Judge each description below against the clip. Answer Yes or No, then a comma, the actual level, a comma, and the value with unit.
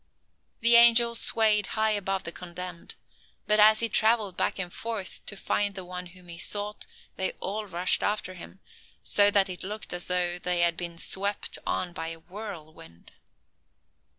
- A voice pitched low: No, high, 190 Hz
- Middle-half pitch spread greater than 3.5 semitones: No, average, 3.0 semitones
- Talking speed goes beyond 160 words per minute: Yes, average, 170 wpm